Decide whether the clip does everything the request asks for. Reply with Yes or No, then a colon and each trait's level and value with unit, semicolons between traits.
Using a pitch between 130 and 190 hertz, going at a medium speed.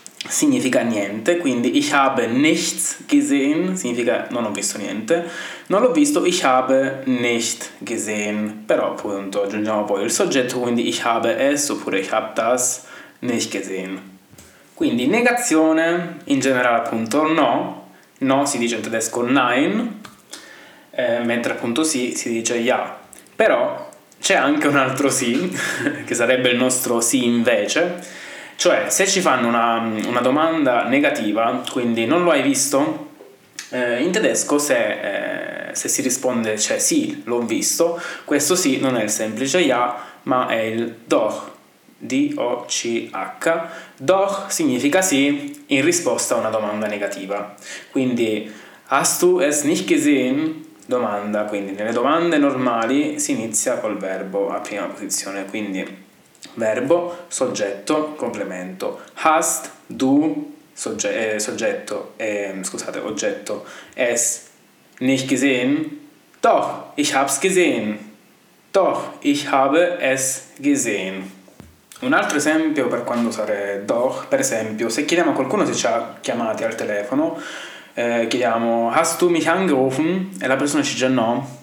Yes: low, 135 Hz; average, 135 wpm